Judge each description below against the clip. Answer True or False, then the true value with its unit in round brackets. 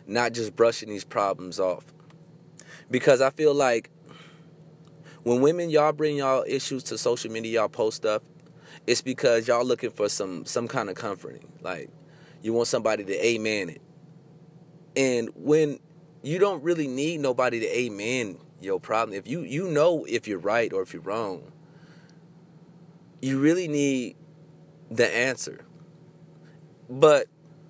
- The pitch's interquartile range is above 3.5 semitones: True (4.4 semitones)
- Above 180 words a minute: False (145 wpm)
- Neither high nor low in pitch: True (155 Hz)